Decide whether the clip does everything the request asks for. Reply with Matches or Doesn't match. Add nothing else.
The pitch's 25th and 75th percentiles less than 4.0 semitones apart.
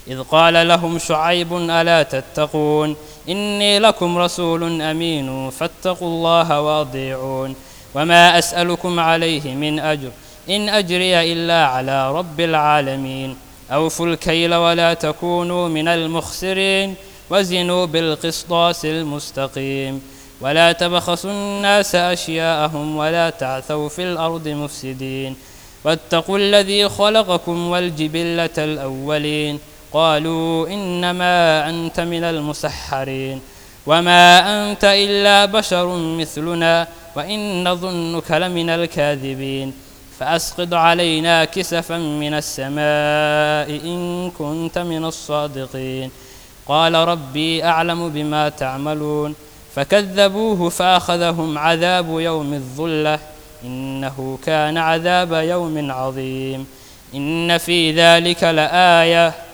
Matches